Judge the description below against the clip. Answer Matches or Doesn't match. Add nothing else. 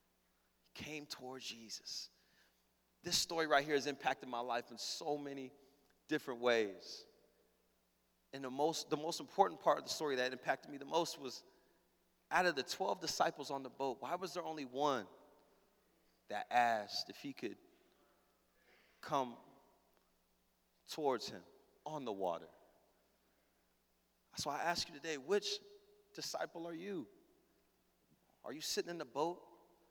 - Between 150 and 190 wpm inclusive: Doesn't match